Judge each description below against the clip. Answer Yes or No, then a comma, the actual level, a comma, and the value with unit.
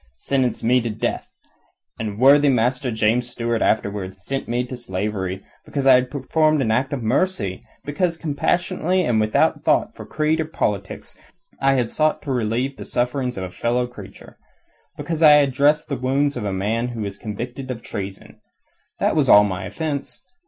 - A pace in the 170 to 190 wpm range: Yes, average, 180 wpm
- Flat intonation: No, average, 4.7 semitones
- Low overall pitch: Yes, low, 125 Hz